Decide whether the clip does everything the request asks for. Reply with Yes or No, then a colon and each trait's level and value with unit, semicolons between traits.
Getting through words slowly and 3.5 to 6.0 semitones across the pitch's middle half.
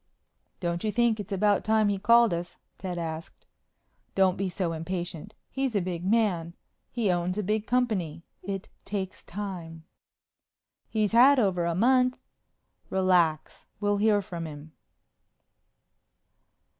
Yes: slow, 130 wpm; average, 3.9 semitones